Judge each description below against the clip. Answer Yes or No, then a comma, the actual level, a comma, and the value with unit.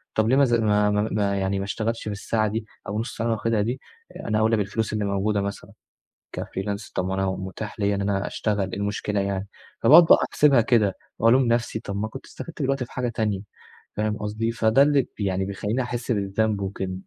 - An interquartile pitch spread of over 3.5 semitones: No, narrow, 2.5 semitones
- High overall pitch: No, low, 105 Hz